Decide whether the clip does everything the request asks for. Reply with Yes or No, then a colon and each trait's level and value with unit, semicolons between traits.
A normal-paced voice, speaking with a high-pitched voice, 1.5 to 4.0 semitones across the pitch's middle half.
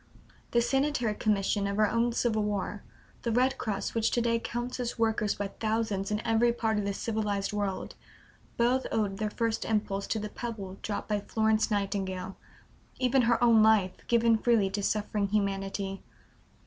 Yes: average, 170 wpm; high, 215 Hz; narrow, 2.5 semitones